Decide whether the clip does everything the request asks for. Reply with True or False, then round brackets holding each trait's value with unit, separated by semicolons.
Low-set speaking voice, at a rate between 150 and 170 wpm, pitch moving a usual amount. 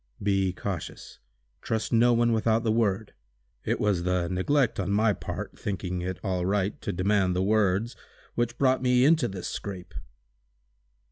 True (100 Hz; 155 wpm; 3.8 semitones)